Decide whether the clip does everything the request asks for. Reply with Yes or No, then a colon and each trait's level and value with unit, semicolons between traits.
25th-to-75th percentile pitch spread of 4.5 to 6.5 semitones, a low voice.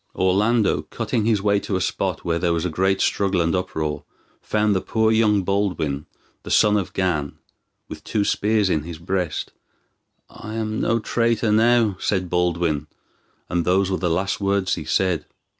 No: average, 3.3 semitones; very low, 95 Hz